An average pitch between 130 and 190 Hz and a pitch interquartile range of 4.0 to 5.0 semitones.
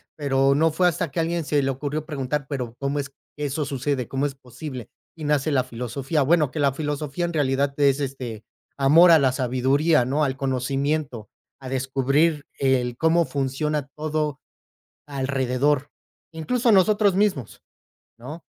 No: medium, 140 Hz; narrow, 2.6 semitones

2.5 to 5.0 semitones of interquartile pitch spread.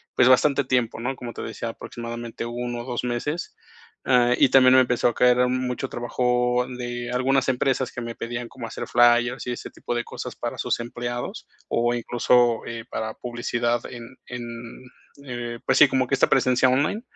No: narrow, 1.1 semitones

